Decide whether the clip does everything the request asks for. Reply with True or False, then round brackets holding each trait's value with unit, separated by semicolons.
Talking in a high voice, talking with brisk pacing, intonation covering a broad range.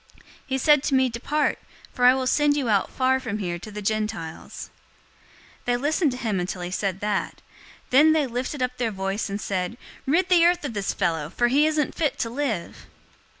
True (245 Hz; 210 wpm; 6.1 semitones)